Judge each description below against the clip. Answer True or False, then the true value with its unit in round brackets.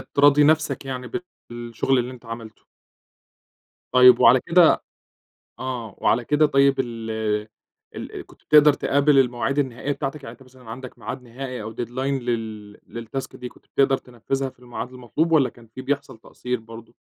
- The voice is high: False (125 Hz)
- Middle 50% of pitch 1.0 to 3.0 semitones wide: True (2.7 semitones)